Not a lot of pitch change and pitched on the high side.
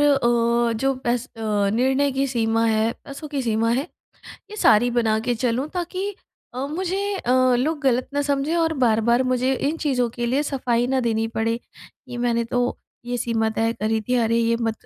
No: average, 3.2 semitones; high, 245 Hz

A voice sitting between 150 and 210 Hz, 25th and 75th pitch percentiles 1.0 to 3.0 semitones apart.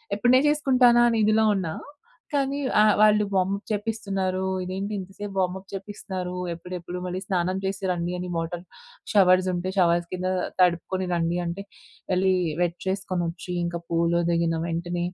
Yes: medium, 185 Hz; average, 2.7 semitones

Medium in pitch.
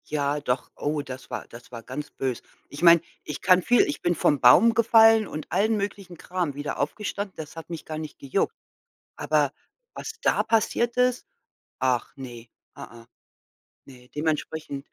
Yes: medium, 155 Hz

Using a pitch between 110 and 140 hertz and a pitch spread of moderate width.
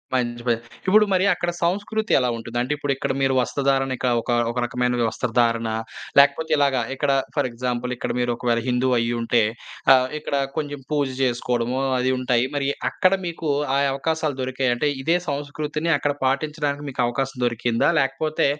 Yes: low, 135 Hz; average, 3.1 semitones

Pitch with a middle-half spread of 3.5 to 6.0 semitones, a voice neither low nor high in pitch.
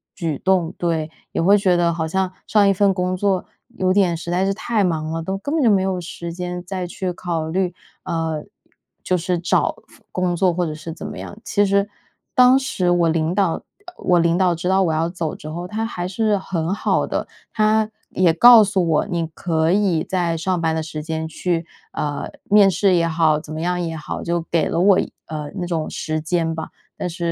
No: average, 2.7 semitones; medium, 175 Hz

